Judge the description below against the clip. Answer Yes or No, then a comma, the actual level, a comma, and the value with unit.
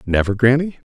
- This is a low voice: Yes, low, 120 Hz